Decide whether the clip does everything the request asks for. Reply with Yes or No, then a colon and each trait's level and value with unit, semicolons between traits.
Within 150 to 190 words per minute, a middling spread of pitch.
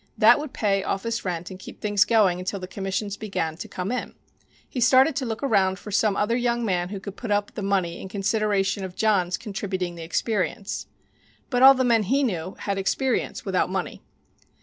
No: average, 200 wpm; average, 3.4 semitones